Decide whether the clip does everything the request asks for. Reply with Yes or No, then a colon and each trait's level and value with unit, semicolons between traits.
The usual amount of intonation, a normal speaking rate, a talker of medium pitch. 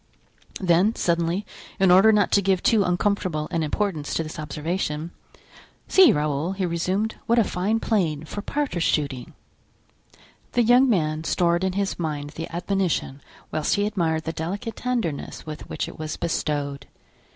Yes: average, 4.6 semitones; average, 155 wpm; medium, 175 Hz